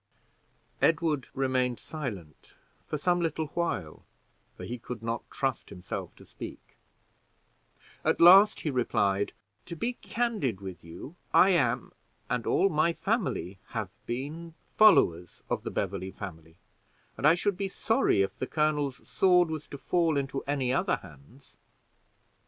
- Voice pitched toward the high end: No, medium, 140 Hz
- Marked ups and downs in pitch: Yes, wide, 8.6 semitones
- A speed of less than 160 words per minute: Yes, average, 140 wpm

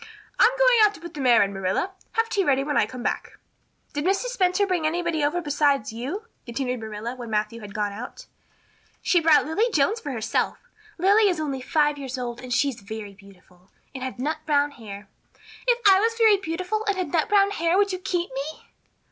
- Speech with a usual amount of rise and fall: No, wide, 7.8 semitones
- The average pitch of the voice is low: No, very high, 295 Hz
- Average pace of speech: No, fast, 210 wpm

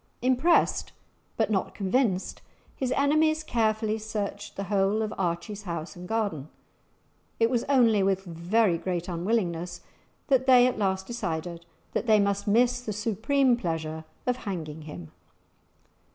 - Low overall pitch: No, high, 205 Hz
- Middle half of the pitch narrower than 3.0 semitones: No, average, 5.2 semitones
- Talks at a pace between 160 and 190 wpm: No, slow, 135 wpm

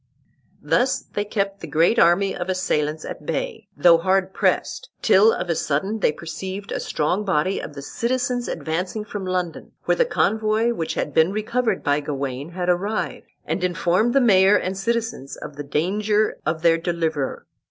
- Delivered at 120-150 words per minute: No, average, 175 wpm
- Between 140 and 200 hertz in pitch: Yes, medium, 185 Hz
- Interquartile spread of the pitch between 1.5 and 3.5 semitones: No, average, 4.7 semitones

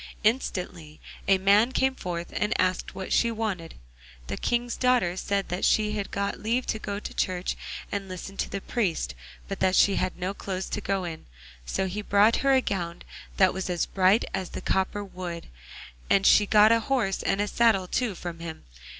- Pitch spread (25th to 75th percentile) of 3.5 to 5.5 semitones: No, average, 2.8 semitones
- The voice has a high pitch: Yes, high, 195 Hz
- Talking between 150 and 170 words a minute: No, average, 195 wpm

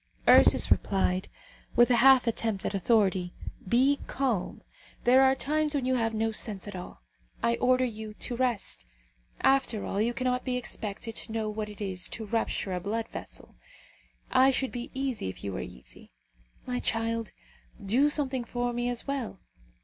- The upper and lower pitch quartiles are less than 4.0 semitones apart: Yes, average, 3.5 semitones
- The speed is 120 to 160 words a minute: No, average, 170 wpm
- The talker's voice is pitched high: Yes, high, 230 Hz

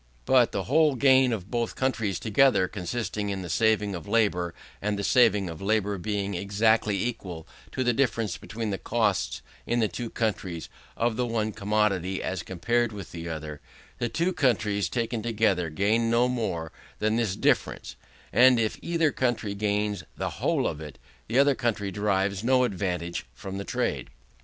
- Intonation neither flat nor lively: Yes, average, 3.7 semitones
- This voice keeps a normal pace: Yes, average, 170 wpm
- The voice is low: Yes, low, 105 Hz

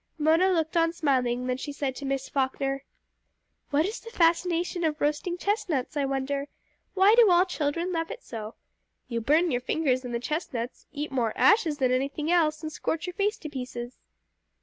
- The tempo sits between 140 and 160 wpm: No, average, 185 wpm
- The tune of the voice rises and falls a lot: No, average, 4.6 semitones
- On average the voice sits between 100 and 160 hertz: No, very high, 300 Hz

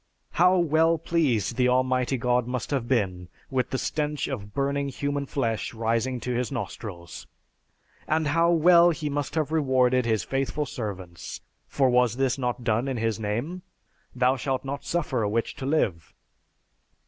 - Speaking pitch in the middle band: No, low, 130 Hz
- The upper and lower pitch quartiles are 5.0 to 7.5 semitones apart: No, average, 3.8 semitones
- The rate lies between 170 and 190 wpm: No, average, 160 wpm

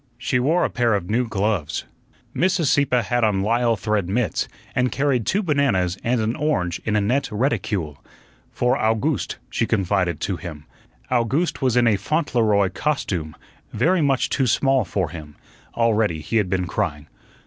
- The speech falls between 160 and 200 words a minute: Yes, average, 165 wpm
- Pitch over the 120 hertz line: No, low, 115 Hz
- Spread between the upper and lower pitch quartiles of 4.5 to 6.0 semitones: Yes, average, 5.3 semitones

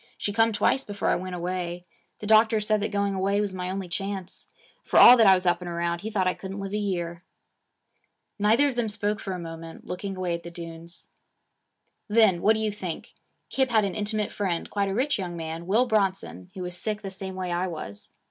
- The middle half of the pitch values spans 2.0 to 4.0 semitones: Yes, average, 3.1 semitones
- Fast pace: Yes, fast, 225 wpm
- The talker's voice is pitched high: Yes, high, 195 Hz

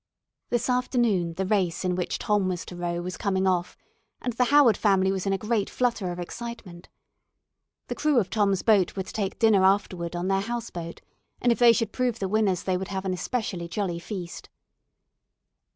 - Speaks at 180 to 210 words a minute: Yes, average, 200 wpm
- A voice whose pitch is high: Yes, high, 195 Hz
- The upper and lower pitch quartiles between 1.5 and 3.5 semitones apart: No, average, 4.0 semitones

